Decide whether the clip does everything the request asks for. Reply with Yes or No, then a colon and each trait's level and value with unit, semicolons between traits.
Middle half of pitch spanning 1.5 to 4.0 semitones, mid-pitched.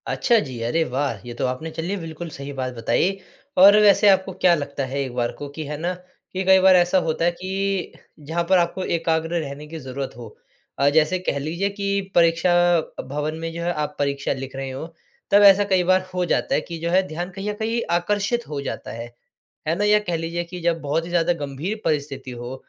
No: average, 4.8 semitones; medium, 165 Hz